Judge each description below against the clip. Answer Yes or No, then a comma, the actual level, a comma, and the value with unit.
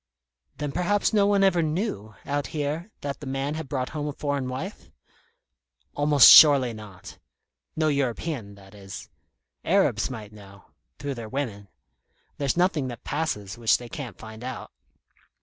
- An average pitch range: No, wide, 5.8 semitones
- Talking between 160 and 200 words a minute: No, average, 150 wpm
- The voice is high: No, medium, 140 Hz